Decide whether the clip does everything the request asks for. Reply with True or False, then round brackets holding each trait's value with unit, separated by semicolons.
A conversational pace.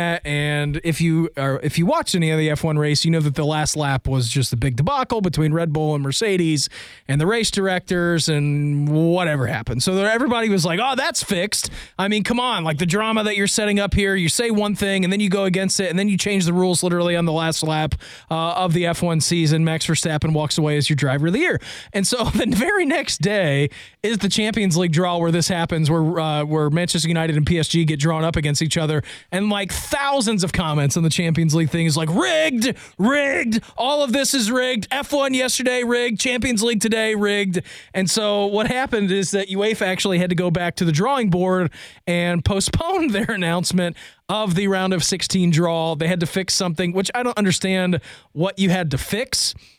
False (220 wpm)